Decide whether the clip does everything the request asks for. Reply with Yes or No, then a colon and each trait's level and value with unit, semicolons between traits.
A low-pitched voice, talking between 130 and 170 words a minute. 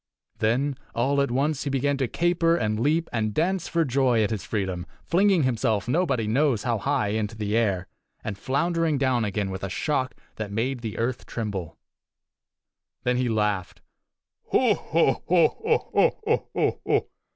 Yes: low, 125 Hz; average, 150 wpm